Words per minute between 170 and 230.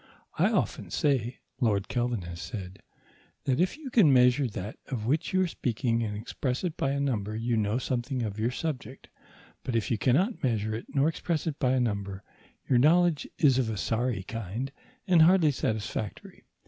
Yes: average, 185 wpm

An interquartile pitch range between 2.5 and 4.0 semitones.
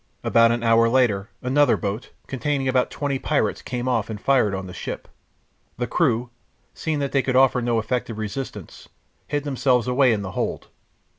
Yes: average, 2.9 semitones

